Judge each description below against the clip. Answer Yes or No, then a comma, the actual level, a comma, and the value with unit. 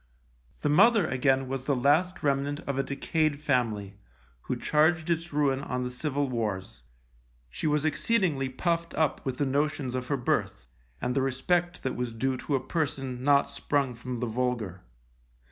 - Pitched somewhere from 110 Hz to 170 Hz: Yes, low, 135 Hz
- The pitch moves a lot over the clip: No, average, 3.1 semitones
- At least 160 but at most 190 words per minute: Yes, average, 170 wpm